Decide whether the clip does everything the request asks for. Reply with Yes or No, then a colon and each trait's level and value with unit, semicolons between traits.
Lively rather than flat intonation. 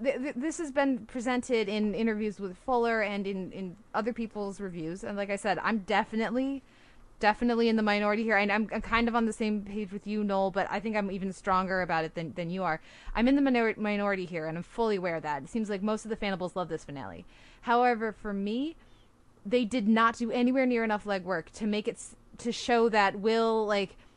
No: average, 2.9 semitones